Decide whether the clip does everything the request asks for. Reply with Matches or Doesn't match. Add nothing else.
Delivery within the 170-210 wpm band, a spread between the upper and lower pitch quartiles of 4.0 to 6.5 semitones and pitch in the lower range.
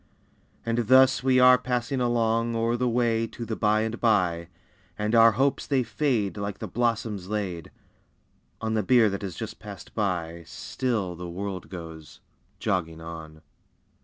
Doesn't match